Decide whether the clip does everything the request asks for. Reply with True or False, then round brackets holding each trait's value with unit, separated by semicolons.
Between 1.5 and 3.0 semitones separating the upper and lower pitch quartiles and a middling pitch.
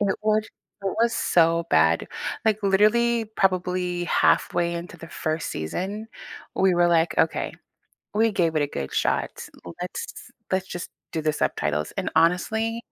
False (4.1 semitones; 180 Hz)